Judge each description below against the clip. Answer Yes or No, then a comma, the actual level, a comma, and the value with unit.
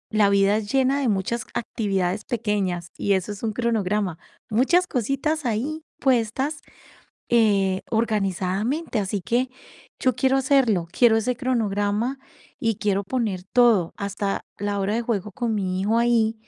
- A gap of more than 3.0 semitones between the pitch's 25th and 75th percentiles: Yes, average, 3.7 semitones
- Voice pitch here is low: No, high, 220 Hz